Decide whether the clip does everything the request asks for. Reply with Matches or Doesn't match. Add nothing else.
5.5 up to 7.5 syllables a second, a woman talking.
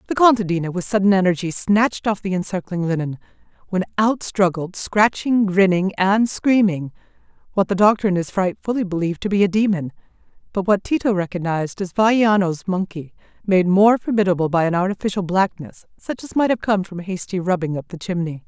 Matches